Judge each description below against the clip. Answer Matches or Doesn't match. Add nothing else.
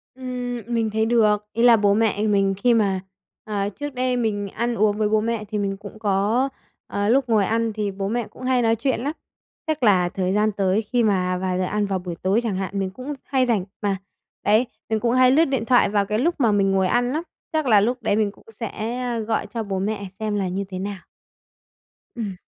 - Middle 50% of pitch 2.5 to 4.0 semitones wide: Matches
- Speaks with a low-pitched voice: Doesn't match